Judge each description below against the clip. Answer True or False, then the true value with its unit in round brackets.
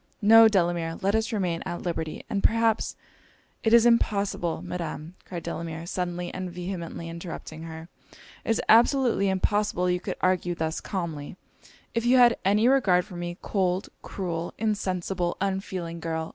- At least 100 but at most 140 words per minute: False (155 wpm)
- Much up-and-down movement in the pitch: False (3.7 semitones)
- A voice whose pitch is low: False (180 Hz)